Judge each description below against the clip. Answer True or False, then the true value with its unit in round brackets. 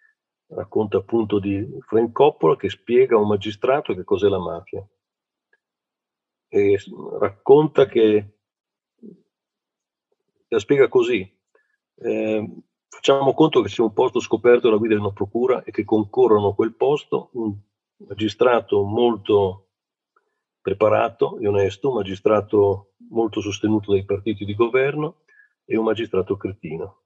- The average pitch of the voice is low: True (130 Hz)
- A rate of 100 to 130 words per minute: True (125 wpm)